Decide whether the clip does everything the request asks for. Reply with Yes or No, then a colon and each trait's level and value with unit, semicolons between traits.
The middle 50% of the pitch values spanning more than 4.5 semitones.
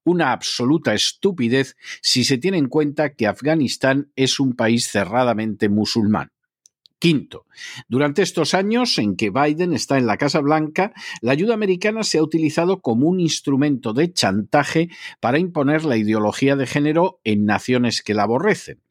Yes: wide, 5.6 semitones